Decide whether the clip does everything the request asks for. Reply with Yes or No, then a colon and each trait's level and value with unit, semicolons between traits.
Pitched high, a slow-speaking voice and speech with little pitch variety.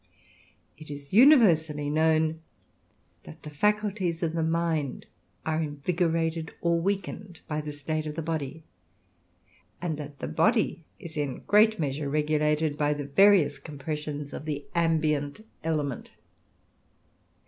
No: medium, 155 Hz; slow, 130 wpm; narrow, 2.3 semitones